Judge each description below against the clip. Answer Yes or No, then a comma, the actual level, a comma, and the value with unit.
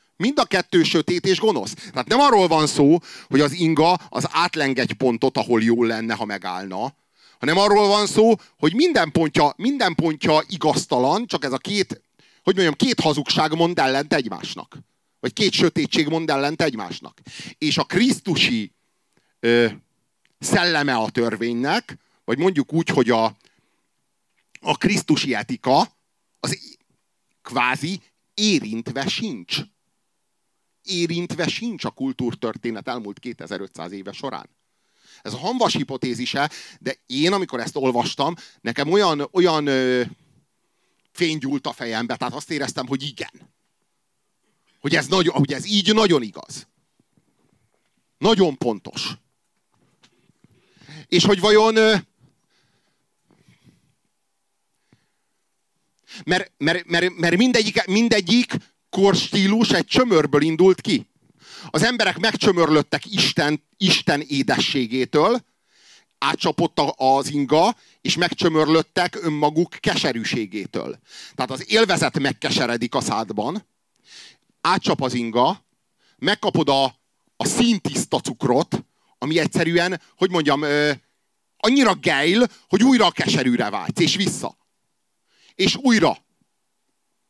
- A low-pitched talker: No, medium, 160 Hz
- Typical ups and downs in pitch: No, wide, 6.0 semitones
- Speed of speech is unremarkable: Yes, average, 115 wpm